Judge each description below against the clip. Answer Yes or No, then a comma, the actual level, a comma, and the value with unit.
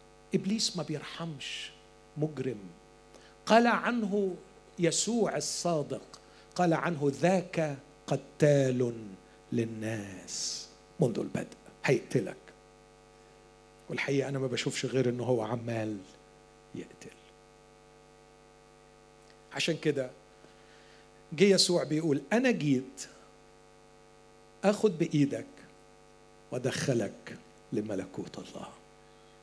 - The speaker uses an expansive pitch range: Yes, wide, 6.1 semitones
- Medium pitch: Yes, medium, 145 Hz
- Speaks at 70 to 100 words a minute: Yes, average, 75 wpm